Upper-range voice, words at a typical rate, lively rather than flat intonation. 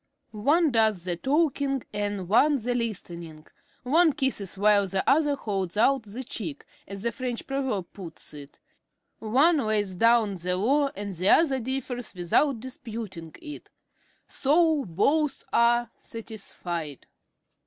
No: high, 225 Hz; slow, 130 wpm; wide, 5.9 semitones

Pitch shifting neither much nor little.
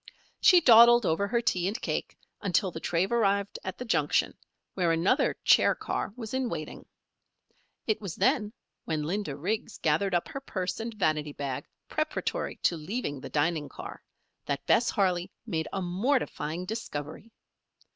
No: wide, 5.8 semitones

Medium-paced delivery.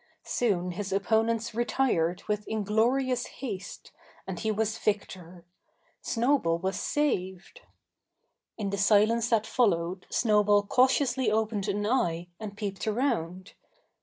No: slow, 115 wpm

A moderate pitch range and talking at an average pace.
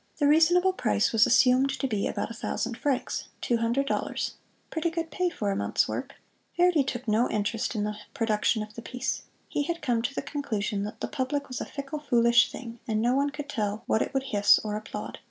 No: average, 4.6 semitones; fast, 220 wpm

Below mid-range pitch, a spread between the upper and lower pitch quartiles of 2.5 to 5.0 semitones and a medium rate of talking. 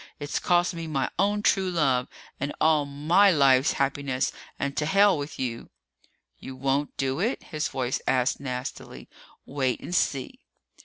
No: medium, 145 Hz; average, 4.1 semitones; average, 160 wpm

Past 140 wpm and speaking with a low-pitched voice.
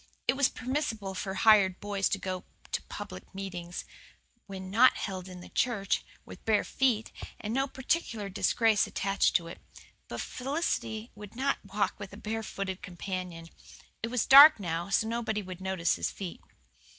No: average, 165 wpm; high, 200 Hz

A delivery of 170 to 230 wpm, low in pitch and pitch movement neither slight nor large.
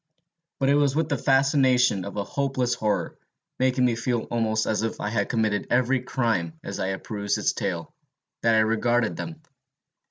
Yes: average, 180 wpm; low, 120 Hz; average, 3.6 semitones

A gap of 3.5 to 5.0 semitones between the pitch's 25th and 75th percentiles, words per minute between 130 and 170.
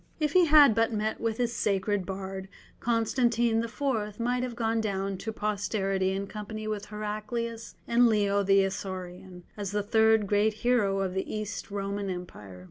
No: narrow, 2.6 semitones; average, 165 wpm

